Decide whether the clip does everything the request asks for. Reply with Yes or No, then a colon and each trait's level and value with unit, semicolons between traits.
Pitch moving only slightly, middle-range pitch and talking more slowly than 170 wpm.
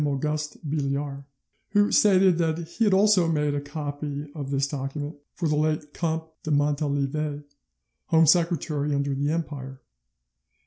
Yes: narrow, 2.2 semitones; medium, 150 Hz; average, 140 wpm